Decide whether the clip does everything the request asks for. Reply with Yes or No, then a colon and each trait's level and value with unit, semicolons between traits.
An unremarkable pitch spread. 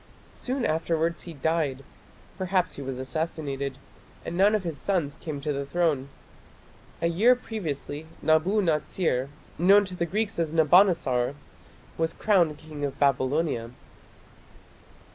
Yes: average, 4.4 semitones